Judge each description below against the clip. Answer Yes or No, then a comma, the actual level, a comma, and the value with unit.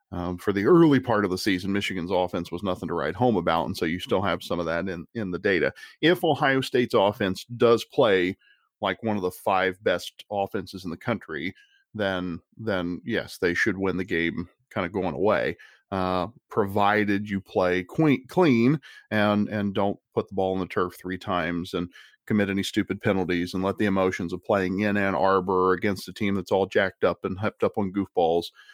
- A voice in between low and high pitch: No, very low, 95 Hz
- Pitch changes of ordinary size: No, narrow, 2.3 semitones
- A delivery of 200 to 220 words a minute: Yes, fast, 205 wpm